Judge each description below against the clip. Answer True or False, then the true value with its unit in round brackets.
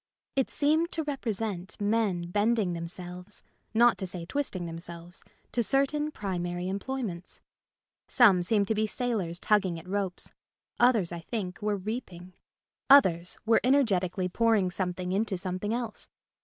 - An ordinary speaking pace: True (145 wpm)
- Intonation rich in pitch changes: False (4.5 semitones)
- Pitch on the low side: False (200 Hz)